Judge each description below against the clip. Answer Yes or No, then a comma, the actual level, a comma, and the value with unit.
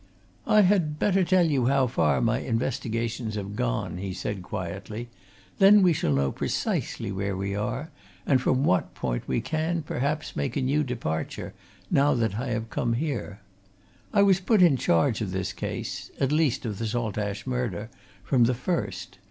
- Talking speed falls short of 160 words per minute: No, average, 175 wpm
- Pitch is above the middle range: No, low, 120 Hz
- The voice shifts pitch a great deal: Yes, wide, 6.6 semitones